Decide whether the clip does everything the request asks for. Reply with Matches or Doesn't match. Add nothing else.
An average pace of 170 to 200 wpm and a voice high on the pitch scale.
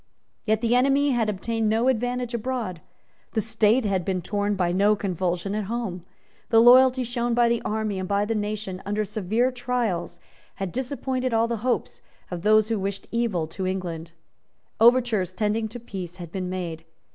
Matches